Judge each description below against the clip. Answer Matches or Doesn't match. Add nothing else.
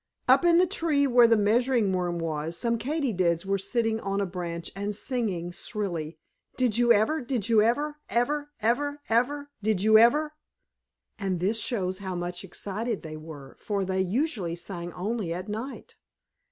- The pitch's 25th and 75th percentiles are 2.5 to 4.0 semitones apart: Doesn't match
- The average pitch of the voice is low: Doesn't match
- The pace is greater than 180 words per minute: Doesn't match